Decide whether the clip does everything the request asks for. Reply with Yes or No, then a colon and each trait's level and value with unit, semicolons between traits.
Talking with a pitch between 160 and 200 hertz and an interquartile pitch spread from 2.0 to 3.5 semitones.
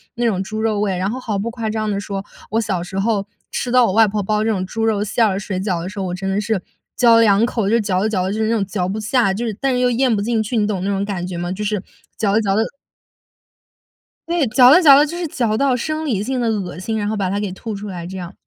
No: high, 210 Hz; average, 3.0 semitones